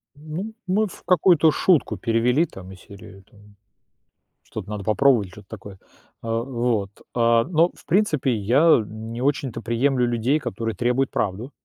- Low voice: Yes, low, 120 Hz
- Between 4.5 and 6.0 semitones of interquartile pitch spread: Yes, average, 5.3 semitones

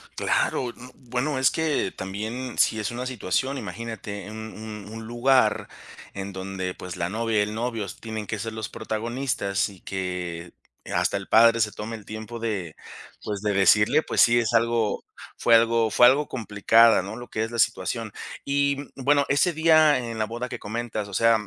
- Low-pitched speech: Yes, low, 115 Hz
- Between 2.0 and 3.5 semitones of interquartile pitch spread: Yes, average, 2.9 semitones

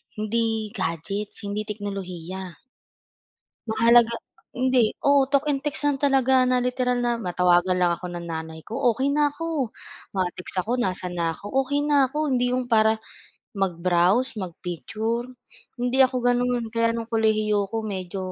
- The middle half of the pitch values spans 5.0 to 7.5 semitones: Yes, average, 5.3 semitones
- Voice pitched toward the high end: Yes, high, 225 Hz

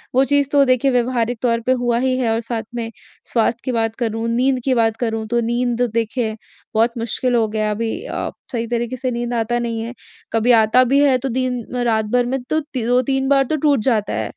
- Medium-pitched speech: No, high, 240 Hz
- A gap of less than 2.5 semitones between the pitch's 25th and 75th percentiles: Yes, narrow, 2.0 semitones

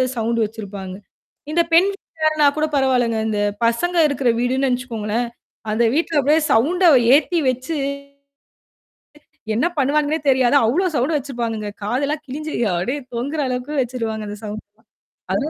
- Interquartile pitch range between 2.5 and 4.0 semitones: No, average, 5.0 semitones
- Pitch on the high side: Yes, very high, 255 Hz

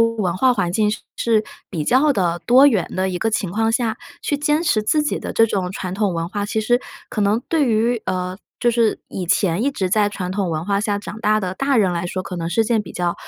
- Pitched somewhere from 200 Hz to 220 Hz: Yes, high, 210 Hz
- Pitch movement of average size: Yes, average, 3.9 semitones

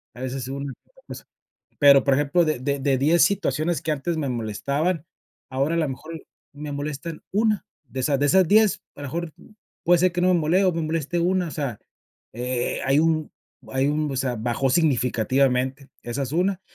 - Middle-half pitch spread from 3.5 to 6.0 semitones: Yes, average, 4.1 semitones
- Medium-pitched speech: Yes, medium, 145 Hz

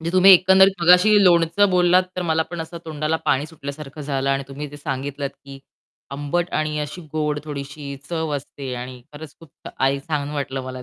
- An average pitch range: Yes, average, 3.3 semitones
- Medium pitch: Yes, medium, 150 Hz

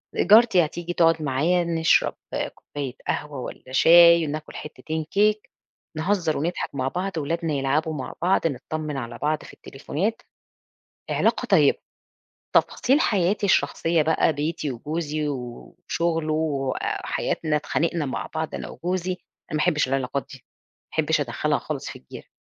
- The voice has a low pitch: No, medium, 155 Hz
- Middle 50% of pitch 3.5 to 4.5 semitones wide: No, average, 3.1 semitones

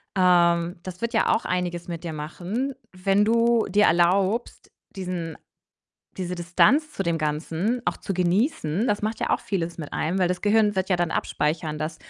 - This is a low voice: No, medium, 180 Hz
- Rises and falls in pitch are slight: No, average, 3.4 semitones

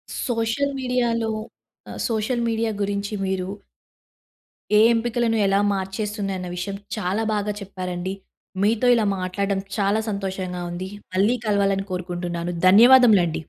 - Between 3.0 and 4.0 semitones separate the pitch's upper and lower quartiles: Yes, average, 3.3 semitones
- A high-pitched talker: Yes, high, 200 Hz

